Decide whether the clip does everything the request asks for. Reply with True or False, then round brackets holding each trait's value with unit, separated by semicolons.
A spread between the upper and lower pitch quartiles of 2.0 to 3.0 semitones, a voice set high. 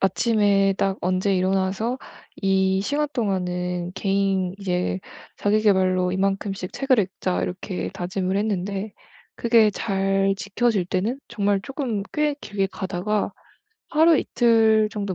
True (2.5 semitones; 195 Hz)